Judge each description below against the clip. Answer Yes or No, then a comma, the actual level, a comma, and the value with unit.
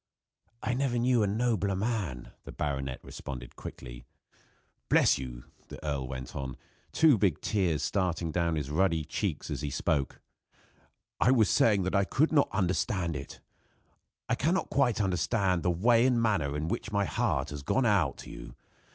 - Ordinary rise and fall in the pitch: No, wide, 7.2 semitones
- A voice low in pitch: Yes, very low, 95 Hz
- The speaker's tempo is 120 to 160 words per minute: No, average, 170 wpm